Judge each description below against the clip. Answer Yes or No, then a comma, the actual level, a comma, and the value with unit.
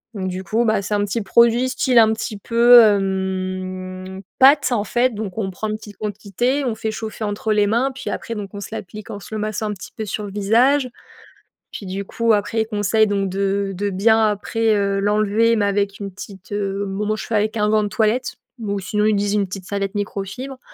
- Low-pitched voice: No, high, 210 Hz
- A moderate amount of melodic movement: No, narrow, 2.0 semitones